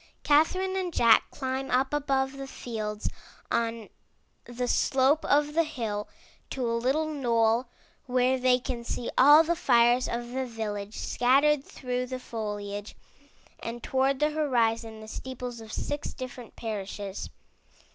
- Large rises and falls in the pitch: No, average, 3.0 semitones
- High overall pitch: Yes, very high, 250 Hz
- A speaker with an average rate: Yes, average, 155 wpm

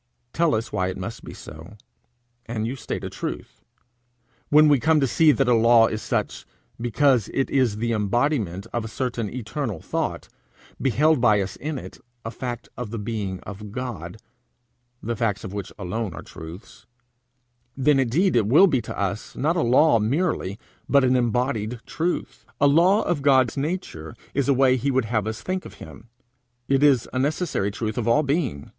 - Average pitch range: Yes, average, 4.8 semitones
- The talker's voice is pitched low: Yes, low, 120 Hz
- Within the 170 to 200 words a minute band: Yes, average, 185 wpm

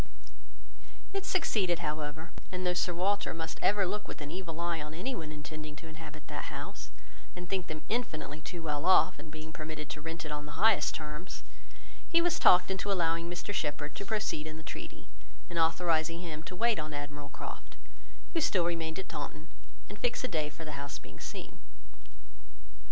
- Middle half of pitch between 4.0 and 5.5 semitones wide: No, average, 3.3 semitones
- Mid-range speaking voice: Yes, medium, 165 Hz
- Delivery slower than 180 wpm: No, average, 190 wpm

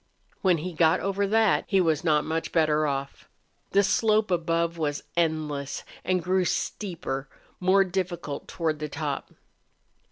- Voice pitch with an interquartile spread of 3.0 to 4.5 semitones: Yes, average, 3.4 semitones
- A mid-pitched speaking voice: Yes, medium, 170 Hz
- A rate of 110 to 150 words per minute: Yes, average, 140 wpm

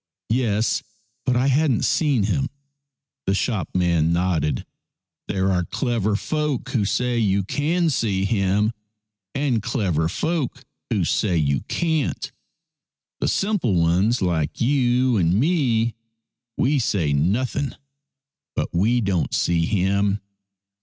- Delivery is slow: Yes, slow, 125 wpm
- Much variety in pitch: Yes, wide, 5.8 semitones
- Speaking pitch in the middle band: No, low, 110 Hz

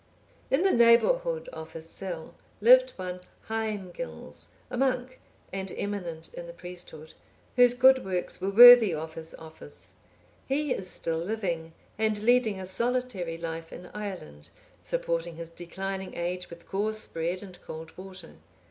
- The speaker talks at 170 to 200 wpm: No, average, 145 wpm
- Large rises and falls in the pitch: Yes, wide, 6.0 semitones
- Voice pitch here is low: No, high, 190 Hz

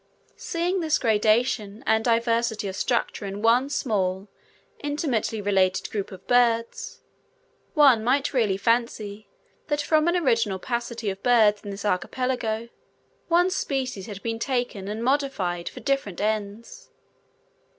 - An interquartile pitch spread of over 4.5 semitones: No, average, 4.1 semitones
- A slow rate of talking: Yes, slow, 130 wpm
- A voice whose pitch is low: No, high, 230 Hz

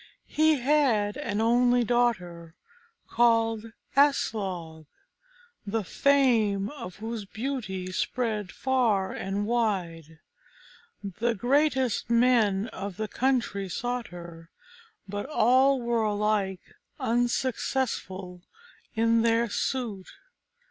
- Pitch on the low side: No, high, 225 Hz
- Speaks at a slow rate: Yes, slow, 95 wpm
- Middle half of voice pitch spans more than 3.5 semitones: Yes, average, 4.0 semitones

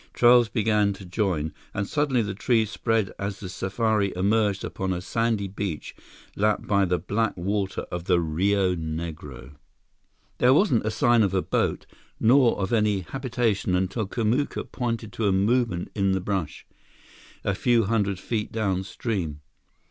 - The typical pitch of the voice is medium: No, low, 100 Hz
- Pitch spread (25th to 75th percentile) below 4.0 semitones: Yes, average, 3.3 semitones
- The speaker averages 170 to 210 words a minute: No, average, 155 wpm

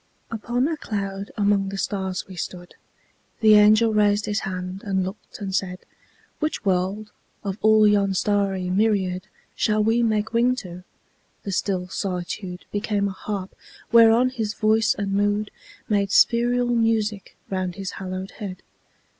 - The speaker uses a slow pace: No, average, 145 wpm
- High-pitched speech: Yes, high, 205 Hz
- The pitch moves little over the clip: Yes, narrow, 2.3 semitones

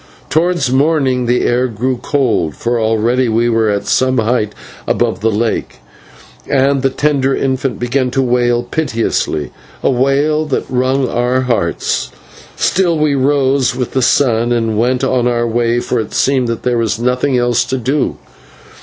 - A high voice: No, low, 125 Hz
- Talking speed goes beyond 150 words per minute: Yes, average, 165 wpm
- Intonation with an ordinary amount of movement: No, narrow, 2.3 semitones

